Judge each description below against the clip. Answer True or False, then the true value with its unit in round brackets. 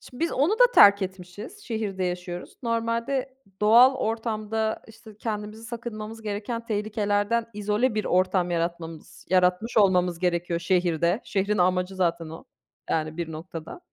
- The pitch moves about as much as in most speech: True (4.0 semitones)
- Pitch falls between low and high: False (205 Hz)